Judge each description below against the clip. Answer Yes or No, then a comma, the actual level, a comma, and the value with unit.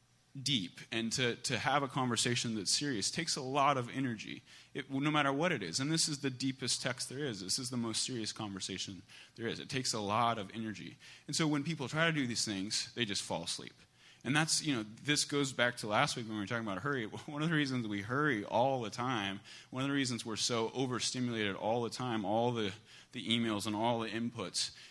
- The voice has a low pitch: Yes, low, 120 Hz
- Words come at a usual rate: No, fast, 240 wpm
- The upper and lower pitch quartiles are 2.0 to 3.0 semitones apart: No, average, 3.6 semitones